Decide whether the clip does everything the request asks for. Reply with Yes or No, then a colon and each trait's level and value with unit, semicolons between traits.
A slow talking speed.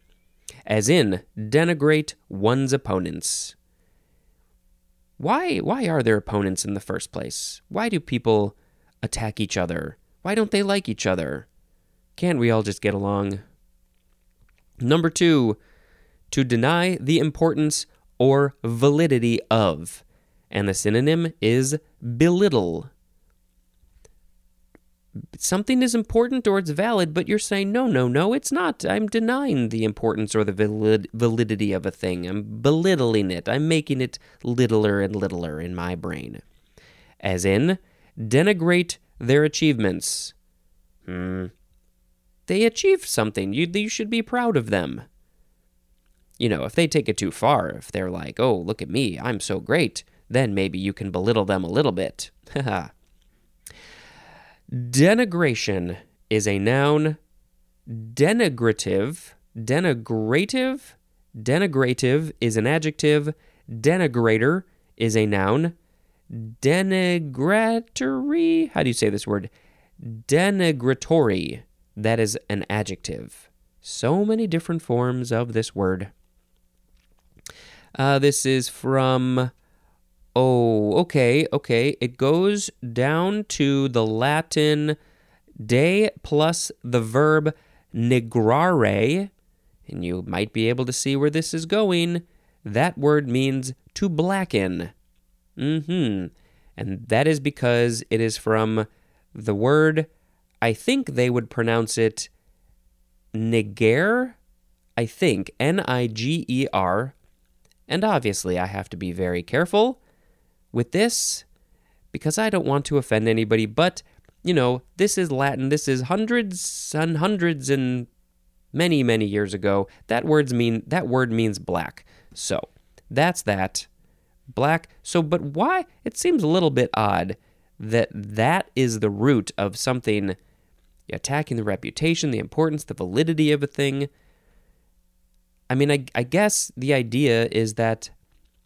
Yes: slow, 125 wpm